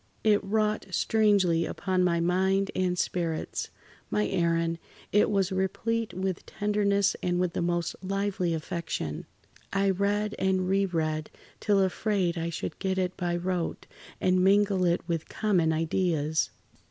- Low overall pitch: No, medium, 185 Hz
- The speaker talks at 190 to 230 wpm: No, average, 140 wpm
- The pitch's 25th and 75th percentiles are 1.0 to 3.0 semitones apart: Yes, average, 2.7 semitones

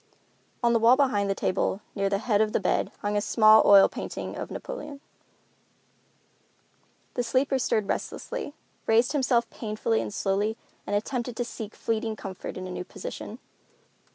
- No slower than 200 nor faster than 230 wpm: No, average, 160 wpm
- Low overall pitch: No, high, 220 Hz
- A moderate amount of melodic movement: Yes, average, 3.2 semitones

